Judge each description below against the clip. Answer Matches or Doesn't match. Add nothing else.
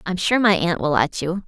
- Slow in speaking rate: Doesn't match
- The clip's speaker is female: Matches